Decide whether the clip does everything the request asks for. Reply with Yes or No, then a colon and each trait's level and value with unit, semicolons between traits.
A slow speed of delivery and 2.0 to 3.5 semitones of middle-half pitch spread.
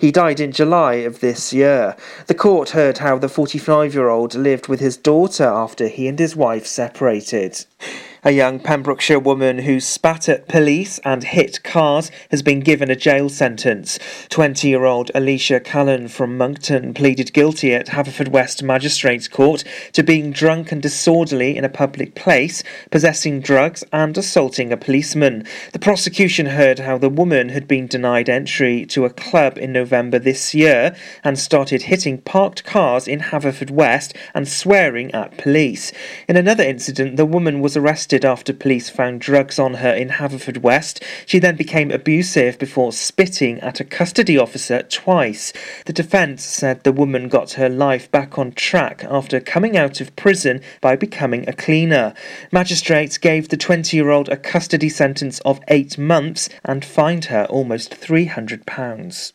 No: average, 165 wpm; average, 3.1 semitones